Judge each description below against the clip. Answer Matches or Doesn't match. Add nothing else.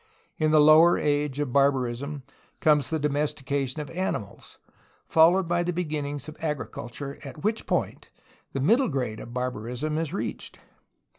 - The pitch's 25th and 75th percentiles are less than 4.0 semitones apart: Matches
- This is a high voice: Doesn't match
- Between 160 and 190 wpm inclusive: Doesn't match